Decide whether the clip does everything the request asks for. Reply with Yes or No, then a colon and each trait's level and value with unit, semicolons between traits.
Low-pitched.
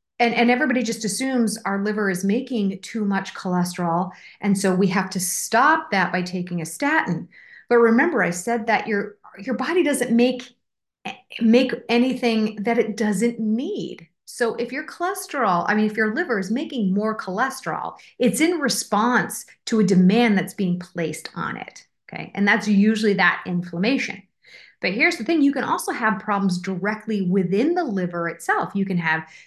No: high, 215 Hz